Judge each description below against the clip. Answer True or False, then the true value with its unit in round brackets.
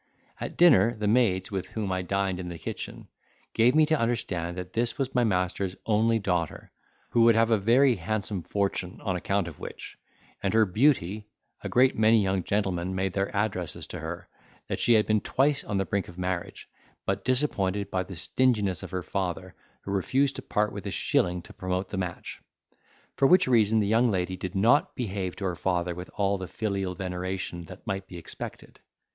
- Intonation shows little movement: False (3.6 semitones)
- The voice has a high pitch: False (100 Hz)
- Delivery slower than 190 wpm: False (195 wpm)